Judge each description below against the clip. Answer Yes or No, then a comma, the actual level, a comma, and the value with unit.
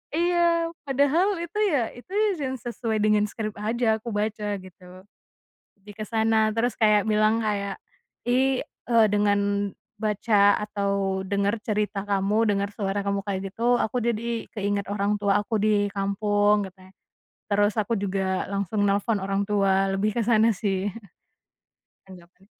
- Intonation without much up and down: Yes, narrow, 2.1 semitones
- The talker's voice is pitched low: No, high, 205 Hz